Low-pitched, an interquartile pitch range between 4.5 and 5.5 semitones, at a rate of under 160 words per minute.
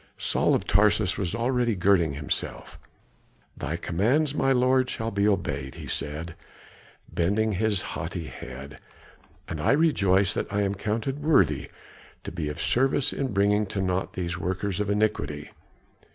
Yes: low, 100 Hz; average, 4.9 semitones; average, 150 wpm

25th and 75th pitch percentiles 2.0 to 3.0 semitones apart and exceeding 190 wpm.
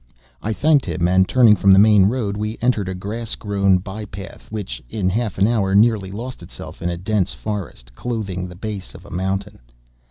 Yes: average, 2.7 semitones; average, 200 wpm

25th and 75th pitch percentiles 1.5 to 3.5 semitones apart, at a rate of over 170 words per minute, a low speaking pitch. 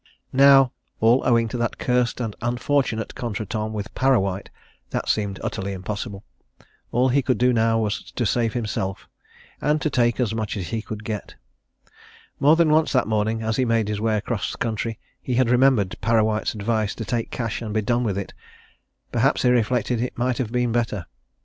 Yes: narrow, 2.6 semitones; average, 185 wpm; low, 115 Hz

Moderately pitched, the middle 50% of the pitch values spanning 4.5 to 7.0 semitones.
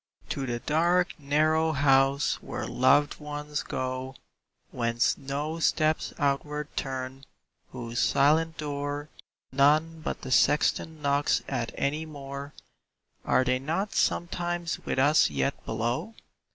No: medium, 145 Hz; average, 2.7 semitones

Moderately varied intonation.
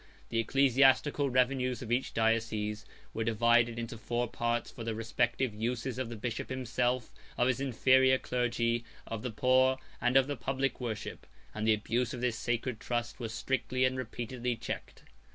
No: narrow, 2.1 semitones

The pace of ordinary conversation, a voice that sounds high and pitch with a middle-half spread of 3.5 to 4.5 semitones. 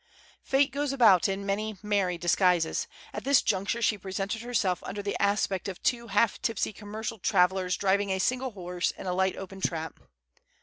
No: average, 175 wpm; high, 200 Hz; average, 3.0 semitones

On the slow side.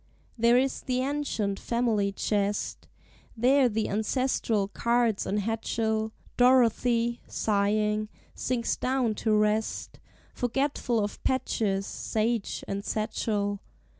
Yes: slow, 105 wpm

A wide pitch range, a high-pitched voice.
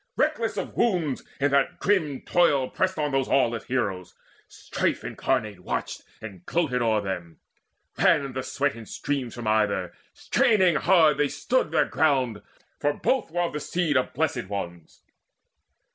No: wide, 6.2 semitones; low, 135 Hz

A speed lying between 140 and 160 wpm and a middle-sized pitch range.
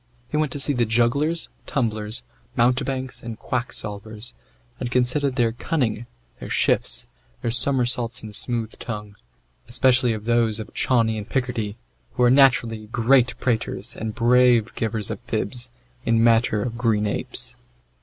No: average, 145 wpm; narrow, 2.3 semitones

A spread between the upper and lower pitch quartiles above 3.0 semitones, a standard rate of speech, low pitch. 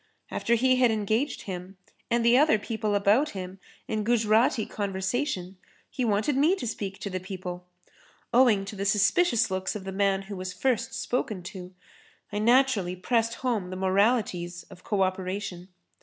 No: average, 3.9 semitones; average, 165 wpm; high, 205 Hz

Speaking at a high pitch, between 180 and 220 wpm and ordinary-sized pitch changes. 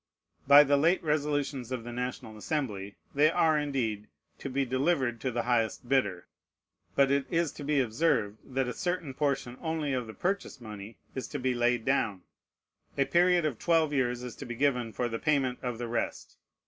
No: low, 130 Hz; average, 190 wpm; average, 3.5 semitones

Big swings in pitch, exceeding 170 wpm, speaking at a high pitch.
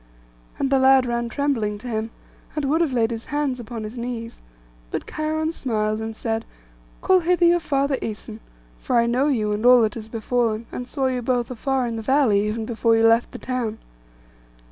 No: average, 3.3 semitones; average, 200 wpm; high, 240 Hz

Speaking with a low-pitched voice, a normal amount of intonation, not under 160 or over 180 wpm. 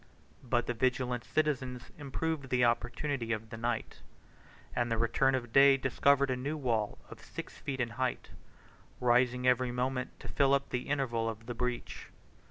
No: low, 125 Hz; narrow, 2.1 semitones; average, 170 wpm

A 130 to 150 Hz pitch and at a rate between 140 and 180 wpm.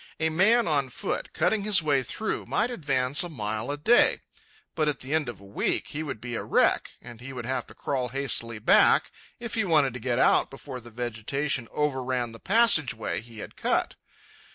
No: low, 135 Hz; fast, 205 wpm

